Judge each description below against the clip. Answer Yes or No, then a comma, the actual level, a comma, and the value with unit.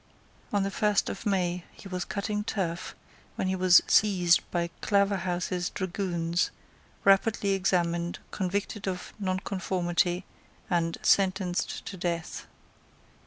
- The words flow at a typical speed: No, slow, 115 wpm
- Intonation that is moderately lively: No, narrow, 2.1 semitones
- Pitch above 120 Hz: Yes, medium, 185 Hz